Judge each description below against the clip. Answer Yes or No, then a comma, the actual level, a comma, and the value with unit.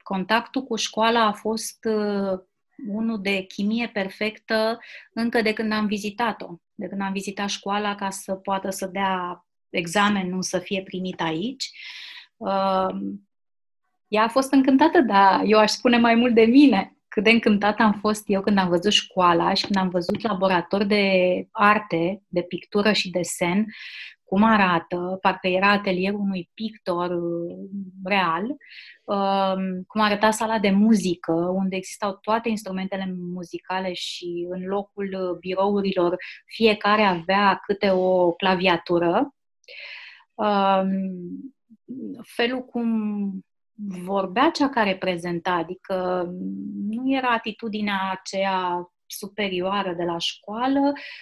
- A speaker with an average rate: Yes, average, 125 wpm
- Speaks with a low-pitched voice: No, high, 195 Hz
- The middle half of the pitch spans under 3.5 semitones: Yes, average, 2.9 semitones